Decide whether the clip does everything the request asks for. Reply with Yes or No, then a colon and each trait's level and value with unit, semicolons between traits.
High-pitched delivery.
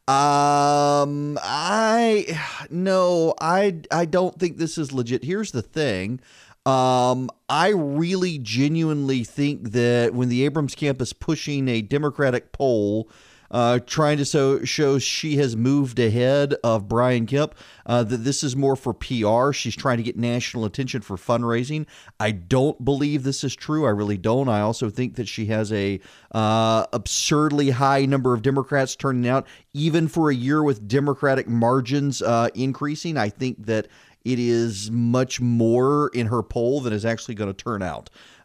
No: low, 135 Hz